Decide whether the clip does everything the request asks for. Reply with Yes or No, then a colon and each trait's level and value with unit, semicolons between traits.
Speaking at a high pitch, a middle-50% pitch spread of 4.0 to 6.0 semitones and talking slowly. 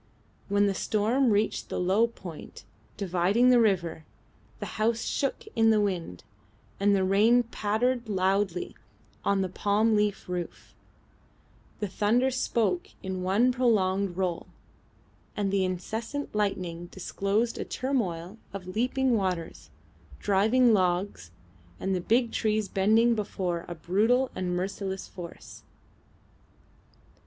No: high, 200 Hz; average, 3.6 semitones; slow, 125 wpm